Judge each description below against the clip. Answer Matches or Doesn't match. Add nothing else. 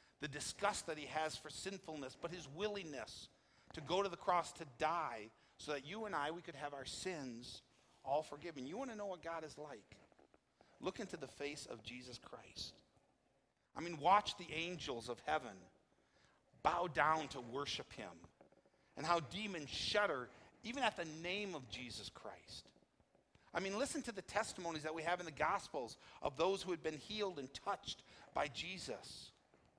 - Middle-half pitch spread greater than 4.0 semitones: Matches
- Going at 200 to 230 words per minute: Doesn't match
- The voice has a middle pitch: Matches